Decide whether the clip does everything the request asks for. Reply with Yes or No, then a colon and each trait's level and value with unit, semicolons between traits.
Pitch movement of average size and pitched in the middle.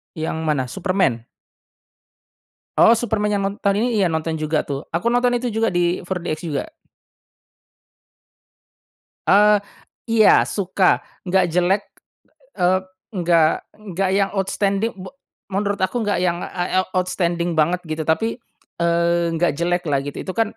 Yes: average, 3.1 semitones; medium, 180 Hz